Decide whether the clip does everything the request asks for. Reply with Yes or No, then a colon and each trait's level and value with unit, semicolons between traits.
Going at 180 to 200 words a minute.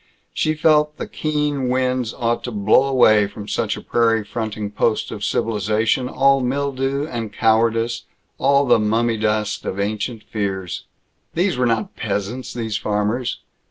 No: average, 155 wpm